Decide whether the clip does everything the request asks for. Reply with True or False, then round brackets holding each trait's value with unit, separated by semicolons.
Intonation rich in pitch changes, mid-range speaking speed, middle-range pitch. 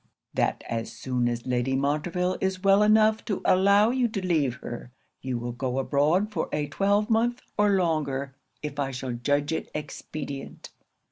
True (6.8 semitones; 160 wpm; 150 Hz)